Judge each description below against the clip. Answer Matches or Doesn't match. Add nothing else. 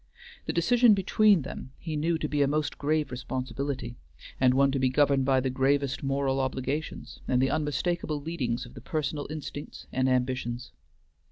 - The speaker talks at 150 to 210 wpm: Matches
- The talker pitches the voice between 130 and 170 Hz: Matches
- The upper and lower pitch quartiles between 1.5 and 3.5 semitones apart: Matches